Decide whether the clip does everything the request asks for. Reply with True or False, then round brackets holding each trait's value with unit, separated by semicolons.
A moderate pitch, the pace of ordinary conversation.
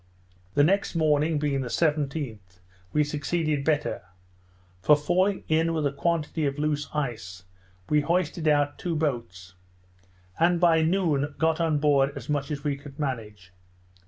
True (150 Hz; 150 wpm)